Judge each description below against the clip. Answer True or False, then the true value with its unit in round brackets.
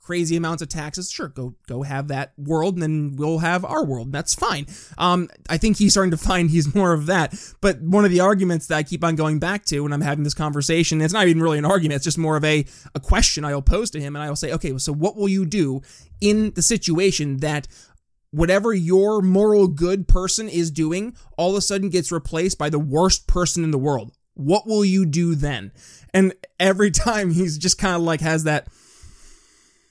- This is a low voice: False (165 Hz)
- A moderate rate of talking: False (225 wpm)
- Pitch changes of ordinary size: True (3.9 semitones)